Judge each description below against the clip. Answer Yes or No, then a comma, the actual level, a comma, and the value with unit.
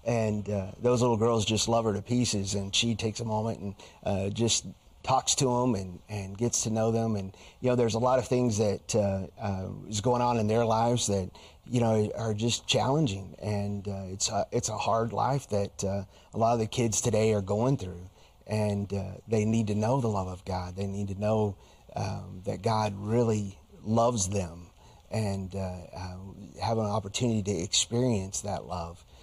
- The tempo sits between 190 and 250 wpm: Yes, fast, 205 wpm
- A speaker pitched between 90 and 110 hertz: Yes, low, 105 Hz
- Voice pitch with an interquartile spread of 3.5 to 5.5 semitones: No, average, 3.0 semitones